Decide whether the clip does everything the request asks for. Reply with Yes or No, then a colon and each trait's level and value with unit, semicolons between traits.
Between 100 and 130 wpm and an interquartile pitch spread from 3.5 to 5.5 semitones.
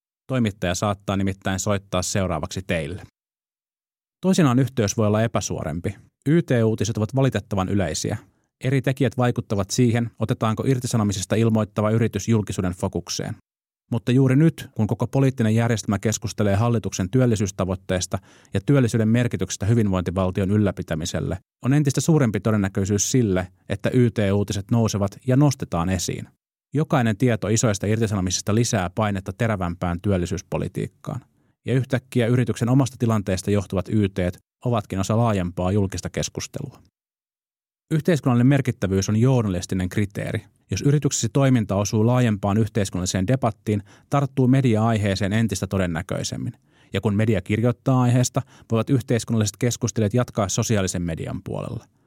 Yes: average, 115 wpm; average, 4.1 semitones